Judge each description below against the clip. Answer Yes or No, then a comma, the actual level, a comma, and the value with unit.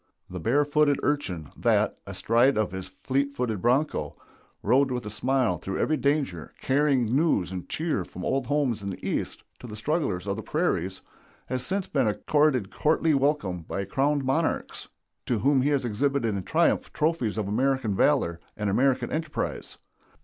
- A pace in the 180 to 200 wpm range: No, average, 165 wpm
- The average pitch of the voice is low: Yes, low, 130 Hz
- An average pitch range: No, wide, 6.0 semitones